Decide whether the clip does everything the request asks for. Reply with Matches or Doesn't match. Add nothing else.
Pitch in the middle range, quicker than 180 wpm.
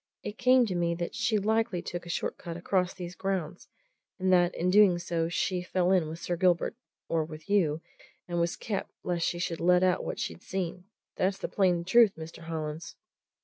Matches